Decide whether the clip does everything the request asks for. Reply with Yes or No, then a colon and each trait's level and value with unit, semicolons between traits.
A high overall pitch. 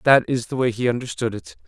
No: low, 120 Hz